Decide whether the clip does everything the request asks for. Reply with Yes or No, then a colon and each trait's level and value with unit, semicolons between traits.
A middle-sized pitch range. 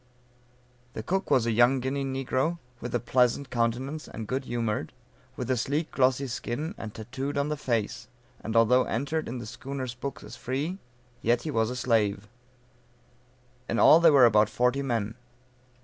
Yes: average, 3.0 semitones